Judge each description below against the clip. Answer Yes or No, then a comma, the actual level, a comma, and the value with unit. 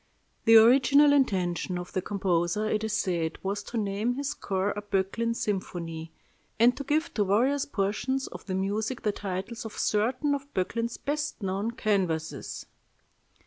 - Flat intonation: No, average, 4.5 semitones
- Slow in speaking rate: No, average, 155 wpm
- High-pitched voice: Yes, high, 210 Hz